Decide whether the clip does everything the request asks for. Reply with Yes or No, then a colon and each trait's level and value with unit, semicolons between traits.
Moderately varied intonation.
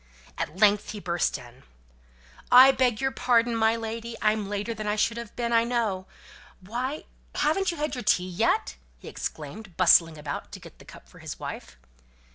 Yes: average, 4.3 semitones